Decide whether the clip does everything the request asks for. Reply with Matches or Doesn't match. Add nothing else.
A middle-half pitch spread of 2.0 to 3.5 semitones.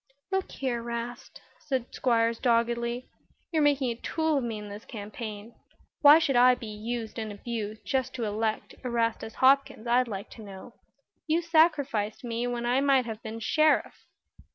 Matches